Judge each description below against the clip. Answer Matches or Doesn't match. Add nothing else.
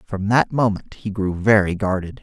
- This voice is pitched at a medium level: Doesn't match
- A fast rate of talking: Doesn't match